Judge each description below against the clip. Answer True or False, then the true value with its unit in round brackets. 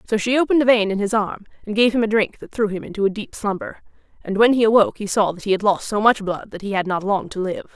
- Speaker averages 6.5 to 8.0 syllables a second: True (6.6 syllables/s)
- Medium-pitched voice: False (210 Hz)